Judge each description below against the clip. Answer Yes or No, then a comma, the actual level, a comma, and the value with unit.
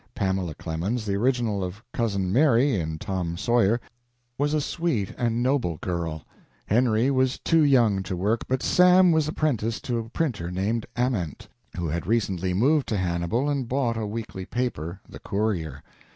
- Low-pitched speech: Yes, low, 110 Hz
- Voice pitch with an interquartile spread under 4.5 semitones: No, wide, 5.6 semitones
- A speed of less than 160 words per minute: No, average, 165 wpm